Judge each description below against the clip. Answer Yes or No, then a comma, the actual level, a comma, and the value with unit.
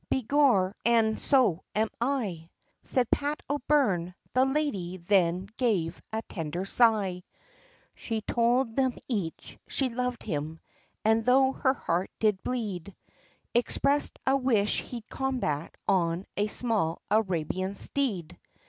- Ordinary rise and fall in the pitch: No, wide, 5.8 semitones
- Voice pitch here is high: Yes, high, 220 Hz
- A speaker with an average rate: No, slow, 120 wpm